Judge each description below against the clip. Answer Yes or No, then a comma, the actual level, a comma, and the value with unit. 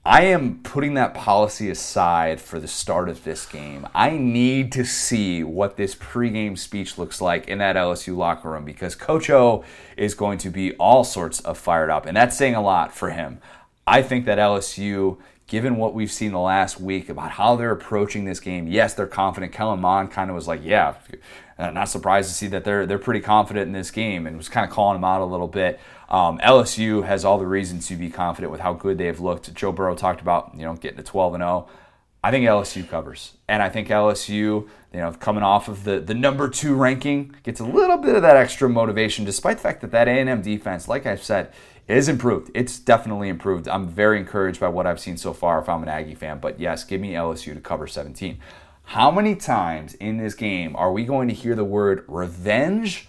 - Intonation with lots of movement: No, average, 3.9 semitones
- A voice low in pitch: Yes, low, 100 Hz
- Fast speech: Yes, fast, 225 wpm